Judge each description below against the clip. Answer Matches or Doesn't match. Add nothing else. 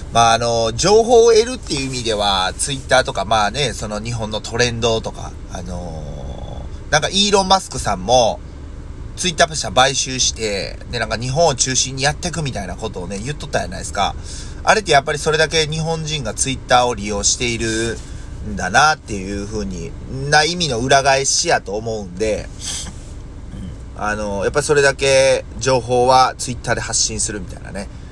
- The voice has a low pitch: Matches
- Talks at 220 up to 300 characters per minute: Doesn't match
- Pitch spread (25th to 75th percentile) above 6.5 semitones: Doesn't match